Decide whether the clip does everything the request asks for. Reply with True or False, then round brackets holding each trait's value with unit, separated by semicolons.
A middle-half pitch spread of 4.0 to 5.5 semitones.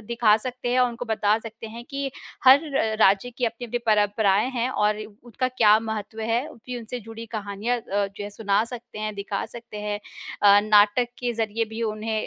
False (2.4 semitones)